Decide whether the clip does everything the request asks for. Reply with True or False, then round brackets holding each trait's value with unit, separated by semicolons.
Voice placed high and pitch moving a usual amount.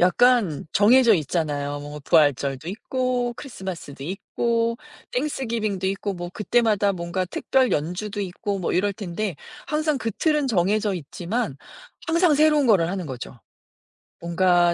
False (195 Hz; 5.7 semitones)